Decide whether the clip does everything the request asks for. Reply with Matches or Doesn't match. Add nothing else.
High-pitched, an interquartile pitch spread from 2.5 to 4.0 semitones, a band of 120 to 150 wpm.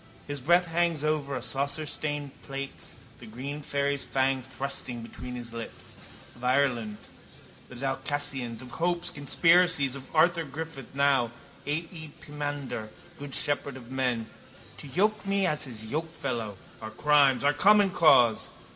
Doesn't match